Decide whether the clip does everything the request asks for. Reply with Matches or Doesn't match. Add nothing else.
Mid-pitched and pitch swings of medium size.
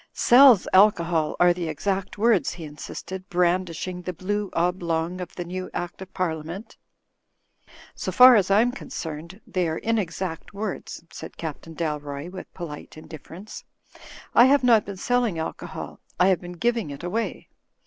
Matches